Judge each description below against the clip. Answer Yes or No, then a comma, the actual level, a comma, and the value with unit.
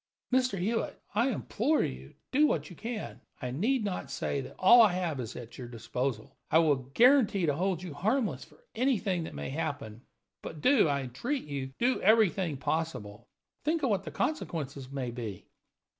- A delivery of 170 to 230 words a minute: Yes, average, 180 wpm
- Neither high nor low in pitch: Yes, medium, 170 Hz